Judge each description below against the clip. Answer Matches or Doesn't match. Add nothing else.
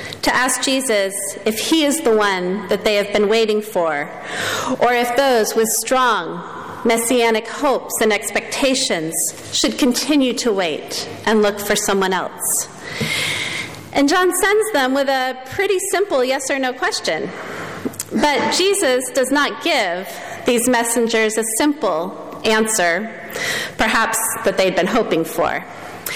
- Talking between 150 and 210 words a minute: Doesn't match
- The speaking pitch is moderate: Doesn't match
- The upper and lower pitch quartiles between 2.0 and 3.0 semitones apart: Doesn't match